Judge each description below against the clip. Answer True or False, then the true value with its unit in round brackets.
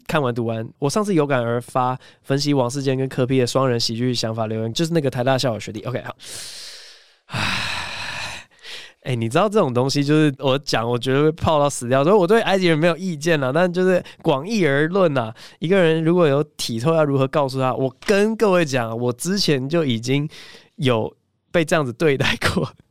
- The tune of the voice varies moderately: True (5.0 semitones)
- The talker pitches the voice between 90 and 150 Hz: True (140 Hz)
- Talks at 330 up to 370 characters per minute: False (300 characters per minute)